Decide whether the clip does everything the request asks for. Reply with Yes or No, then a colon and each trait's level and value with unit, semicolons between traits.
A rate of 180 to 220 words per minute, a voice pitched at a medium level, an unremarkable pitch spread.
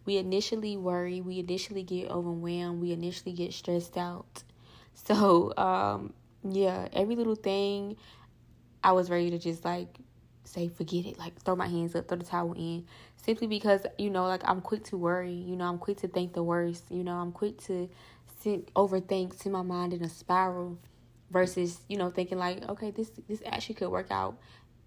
No: average, 190 wpm; medium, 180 Hz; narrow, 2.0 semitones